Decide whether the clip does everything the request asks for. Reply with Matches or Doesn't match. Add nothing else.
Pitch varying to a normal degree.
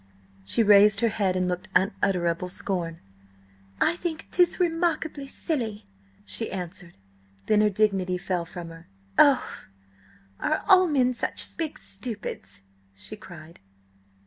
Doesn't match